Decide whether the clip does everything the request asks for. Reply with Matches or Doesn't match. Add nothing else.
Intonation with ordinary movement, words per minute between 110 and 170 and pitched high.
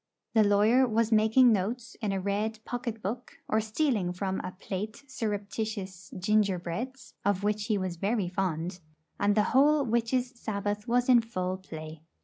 Matches